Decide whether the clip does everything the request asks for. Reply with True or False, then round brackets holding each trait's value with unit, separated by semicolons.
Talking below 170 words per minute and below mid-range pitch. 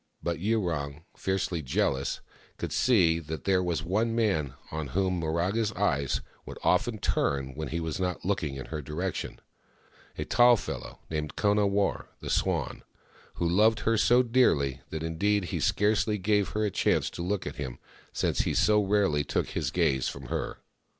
False (180 wpm; 90 Hz)